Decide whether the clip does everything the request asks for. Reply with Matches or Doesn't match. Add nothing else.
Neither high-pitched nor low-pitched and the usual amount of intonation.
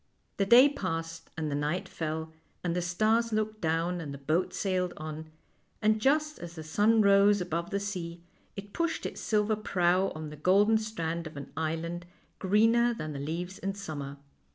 Matches